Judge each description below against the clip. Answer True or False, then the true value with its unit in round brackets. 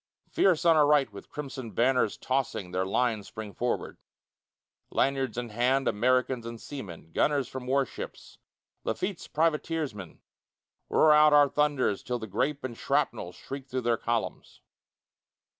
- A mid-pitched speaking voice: False (130 Hz)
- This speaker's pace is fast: False (140 wpm)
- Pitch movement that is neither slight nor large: True (4.3 semitones)